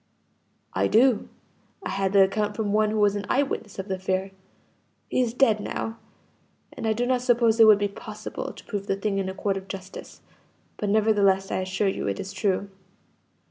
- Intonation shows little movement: Yes, narrow, 2.2 semitones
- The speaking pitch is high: Yes, high, 205 Hz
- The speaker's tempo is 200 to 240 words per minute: Yes, fast, 205 wpm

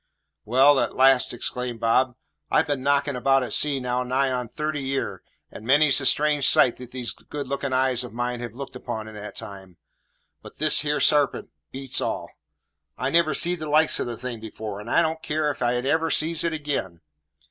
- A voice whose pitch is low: Yes, low, 130 Hz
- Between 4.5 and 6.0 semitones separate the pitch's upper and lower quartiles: No, average, 3.2 semitones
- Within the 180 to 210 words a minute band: Yes, average, 200 wpm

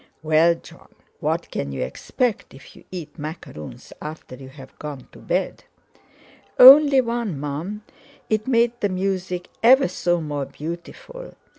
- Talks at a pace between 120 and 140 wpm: Yes, slow, 135 wpm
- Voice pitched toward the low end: No, medium, 175 Hz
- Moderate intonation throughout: No, wide, 7.7 semitones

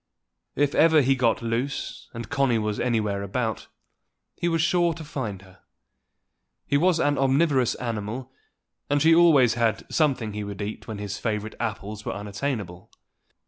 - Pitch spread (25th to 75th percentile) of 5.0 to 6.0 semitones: Yes, average, 5.3 semitones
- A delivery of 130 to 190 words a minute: Yes, average, 155 wpm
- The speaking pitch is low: Yes, low, 120 Hz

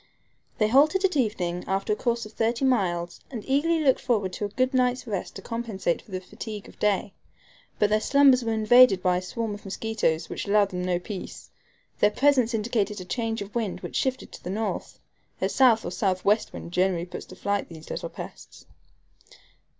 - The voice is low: No, high, 215 Hz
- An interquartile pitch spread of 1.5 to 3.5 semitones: No, average, 4.3 semitones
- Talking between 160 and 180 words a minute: No, average, 195 wpm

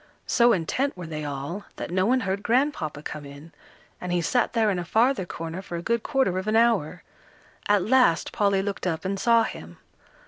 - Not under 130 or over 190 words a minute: No, fast, 205 wpm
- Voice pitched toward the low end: No, high, 190 Hz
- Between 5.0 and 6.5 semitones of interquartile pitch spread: Yes, wide, 5.6 semitones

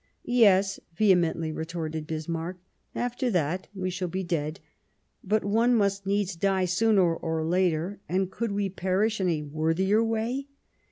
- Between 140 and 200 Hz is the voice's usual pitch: Yes, medium, 185 Hz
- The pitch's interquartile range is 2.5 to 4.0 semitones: Yes, average, 3.6 semitones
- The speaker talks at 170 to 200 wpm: No, average, 145 wpm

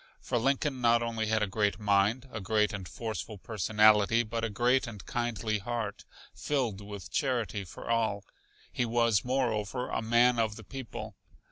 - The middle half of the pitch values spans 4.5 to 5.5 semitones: No, narrow, 2.4 semitones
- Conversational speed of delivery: Yes, average, 165 wpm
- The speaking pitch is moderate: No, low, 115 Hz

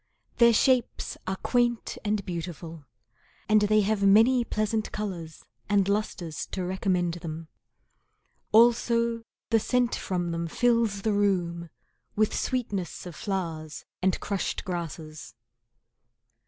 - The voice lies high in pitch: Yes, high, 200 Hz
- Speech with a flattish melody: No, average, 4.4 semitones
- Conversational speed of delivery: No, slow, 115 wpm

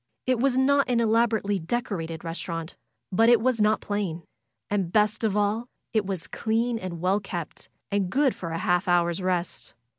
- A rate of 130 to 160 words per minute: No, average, 175 wpm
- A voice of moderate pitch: No, high, 205 Hz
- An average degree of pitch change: Yes, average, 4.5 semitones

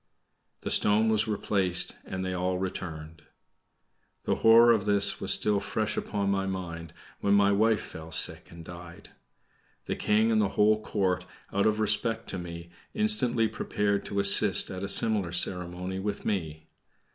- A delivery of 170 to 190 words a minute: No, average, 160 wpm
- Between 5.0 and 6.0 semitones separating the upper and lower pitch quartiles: No, average, 3.1 semitones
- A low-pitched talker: Yes, low, 100 Hz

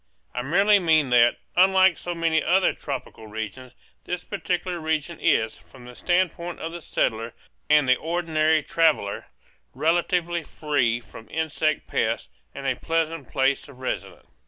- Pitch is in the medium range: Yes, medium, 155 Hz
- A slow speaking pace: No, average, 145 wpm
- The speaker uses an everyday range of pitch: Yes, average, 4.9 semitones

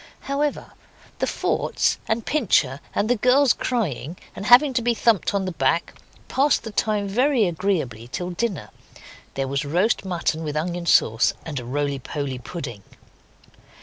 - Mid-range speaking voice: Yes, medium, 180 Hz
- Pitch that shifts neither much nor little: No, wide, 8.4 semitones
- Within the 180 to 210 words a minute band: No, average, 155 wpm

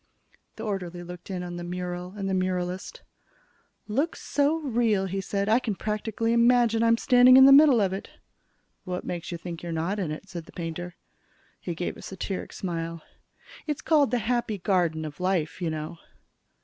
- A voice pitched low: No, high, 190 Hz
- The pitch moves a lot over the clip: No, average, 4.7 semitones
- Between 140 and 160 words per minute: No, average, 185 wpm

